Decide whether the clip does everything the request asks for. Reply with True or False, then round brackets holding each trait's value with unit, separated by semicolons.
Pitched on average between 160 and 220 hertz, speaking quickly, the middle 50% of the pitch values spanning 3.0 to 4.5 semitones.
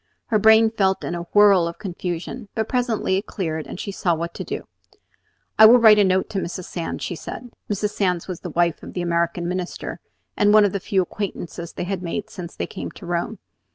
True (190 Hz; 225 wpm; 3.4 semitones)